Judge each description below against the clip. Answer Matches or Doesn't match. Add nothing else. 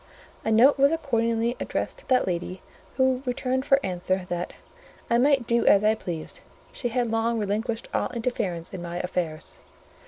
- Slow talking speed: Doesn't match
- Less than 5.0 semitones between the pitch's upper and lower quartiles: Doesn't match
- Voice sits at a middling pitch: Doesn't match